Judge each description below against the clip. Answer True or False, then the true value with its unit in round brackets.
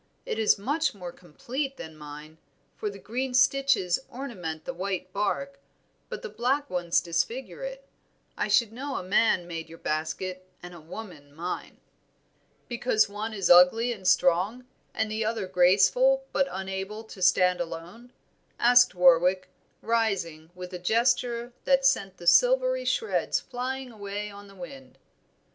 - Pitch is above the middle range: True (205 Hz)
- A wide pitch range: True (5.8 semitones)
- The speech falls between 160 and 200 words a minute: False (150 wpm)